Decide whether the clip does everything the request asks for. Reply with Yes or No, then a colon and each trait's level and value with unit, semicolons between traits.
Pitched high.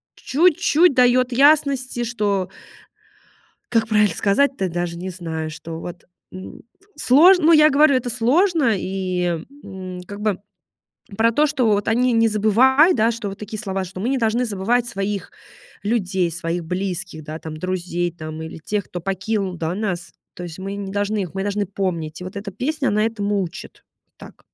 Yes: high, 205 Hz